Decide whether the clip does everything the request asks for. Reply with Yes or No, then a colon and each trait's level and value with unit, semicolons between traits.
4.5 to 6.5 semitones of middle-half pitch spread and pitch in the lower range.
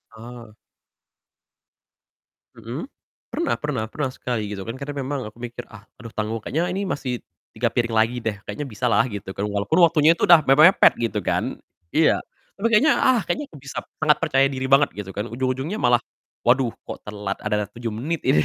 Yes: average, 5.3 semitones; low, 125 Hz